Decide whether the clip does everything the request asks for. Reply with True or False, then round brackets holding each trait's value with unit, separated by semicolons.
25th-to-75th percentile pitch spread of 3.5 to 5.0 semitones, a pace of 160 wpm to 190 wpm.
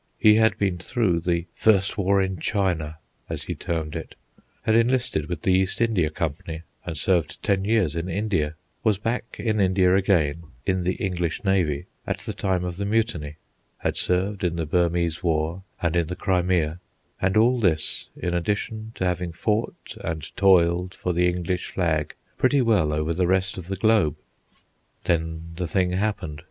False (3.1 semitones; 175 wpm)